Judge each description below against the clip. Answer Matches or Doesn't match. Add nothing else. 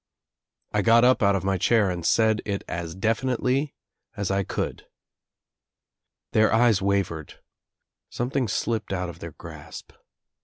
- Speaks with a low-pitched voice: Matches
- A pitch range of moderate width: Matches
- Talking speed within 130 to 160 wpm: Matches